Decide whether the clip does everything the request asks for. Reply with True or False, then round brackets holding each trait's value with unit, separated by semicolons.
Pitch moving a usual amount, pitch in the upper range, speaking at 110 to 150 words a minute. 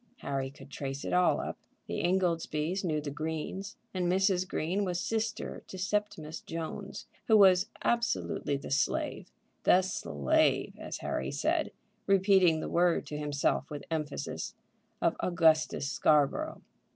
False (4.3 semitones; 170 Hz; 140 wpm)